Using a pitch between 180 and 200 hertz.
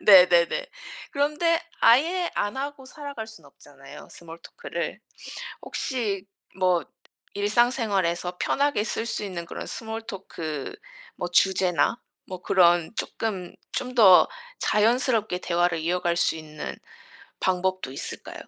Yes: high, 195 Hz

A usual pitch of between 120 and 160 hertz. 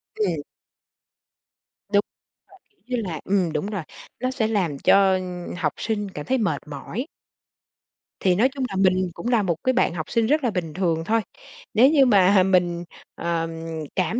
No: high, 195 Hz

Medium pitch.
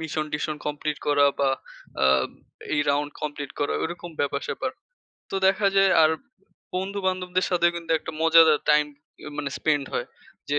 Yes: medium, 155 Hz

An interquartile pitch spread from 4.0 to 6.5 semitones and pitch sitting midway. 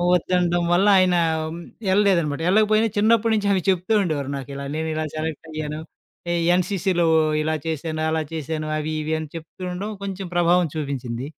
No: average, 3.2 semitones; medium, 170 Hz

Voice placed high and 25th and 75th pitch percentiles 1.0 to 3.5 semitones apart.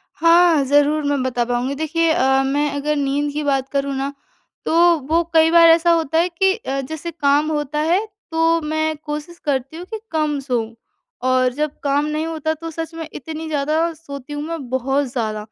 Yes: very high, 300 Hz; average, 2.9 semitones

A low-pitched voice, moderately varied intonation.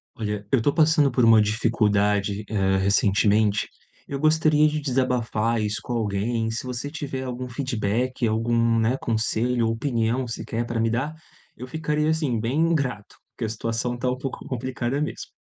Yes: low, 120 Hz; average, 3.2 semitones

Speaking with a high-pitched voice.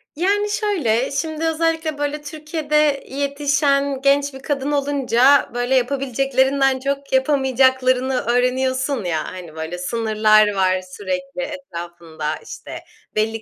Yes: very high, 270 Hz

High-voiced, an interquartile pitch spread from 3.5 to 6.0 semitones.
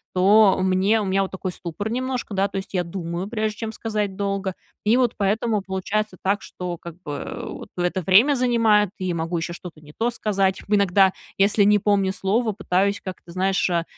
No: high, 195 Hz; narrow, 2.4 semitones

